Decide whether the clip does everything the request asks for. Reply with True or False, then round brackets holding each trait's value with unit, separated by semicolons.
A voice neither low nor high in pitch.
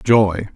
False (100 Hz)